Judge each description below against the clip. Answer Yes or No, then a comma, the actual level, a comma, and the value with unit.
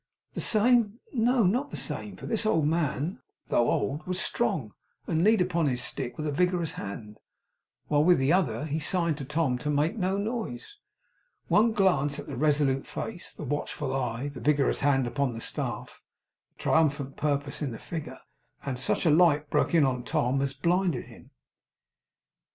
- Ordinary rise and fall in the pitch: Yes, average, 5.0 semitones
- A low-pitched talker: No, medium, 150 Hz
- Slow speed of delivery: No, average, 180 wpm